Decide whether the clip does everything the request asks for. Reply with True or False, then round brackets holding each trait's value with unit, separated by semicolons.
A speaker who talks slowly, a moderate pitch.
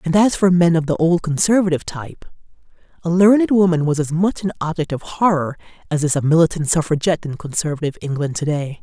False (195 wpm; 165 Hz)